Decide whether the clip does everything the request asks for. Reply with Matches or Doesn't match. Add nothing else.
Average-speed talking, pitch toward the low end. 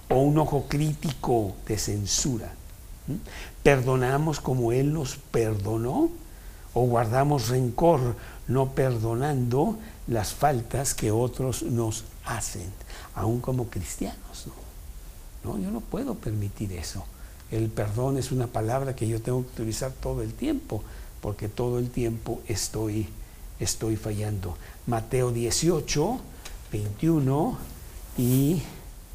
Doesn't match